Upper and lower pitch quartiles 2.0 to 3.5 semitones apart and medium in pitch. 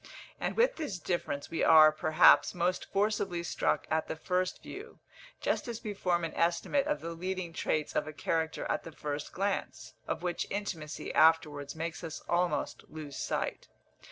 Yes: average, 3.2 semitones; medium, 170 Hz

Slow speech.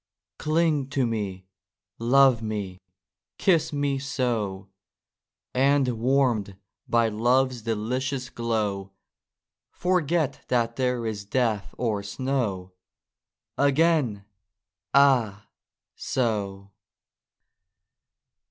Yes: slow, 80 wpm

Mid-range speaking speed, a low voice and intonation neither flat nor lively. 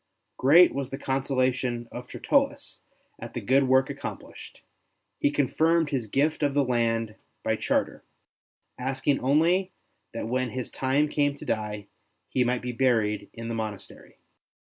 Yes: average, 145 wpm; low, 130 Hz; average, 3.1 semitones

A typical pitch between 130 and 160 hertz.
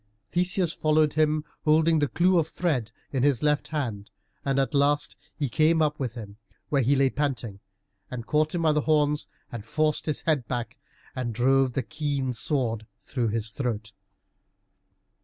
Yes: medium, 140 Hz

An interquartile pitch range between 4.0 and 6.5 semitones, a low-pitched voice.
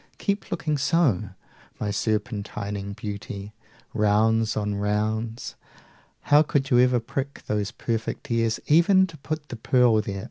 Yes: average, 4.5 semitones; low, 110 Hz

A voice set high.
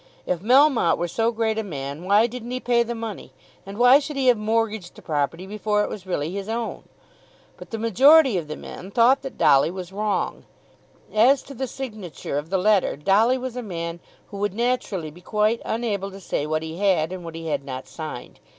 Yes: high, 210 Hz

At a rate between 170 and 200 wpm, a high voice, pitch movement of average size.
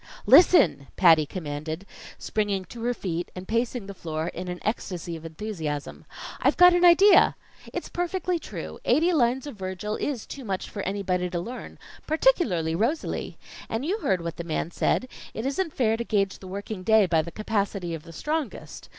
No: average, 180 wpm; high, 200 Hz; wide, 6.6 semitones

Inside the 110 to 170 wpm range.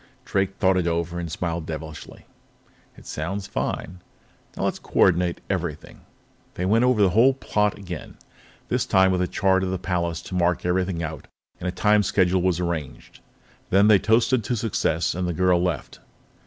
No: average, 180 wpm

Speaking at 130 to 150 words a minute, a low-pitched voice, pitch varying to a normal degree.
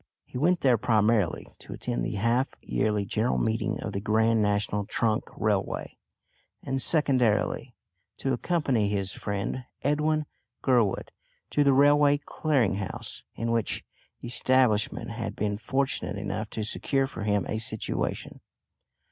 Yes: average, 140 wpm; low, 115 Hz; average, 4.4 semitones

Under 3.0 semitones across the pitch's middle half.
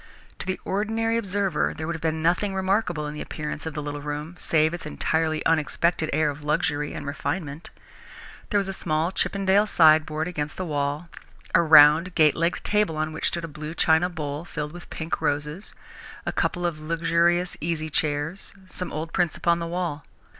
Yes: narrow, 2.6 semitones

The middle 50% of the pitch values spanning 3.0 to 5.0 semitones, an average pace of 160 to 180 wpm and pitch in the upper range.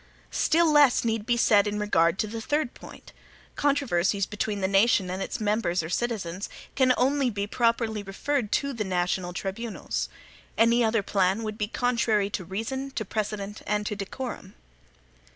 Yes: average, 3.3 semitones; average, 165 wpm; high, 215 Hz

